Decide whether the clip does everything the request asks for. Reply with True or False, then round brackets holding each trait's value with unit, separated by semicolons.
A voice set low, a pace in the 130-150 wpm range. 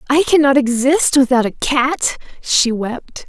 False (265 Hz; 145 wpm)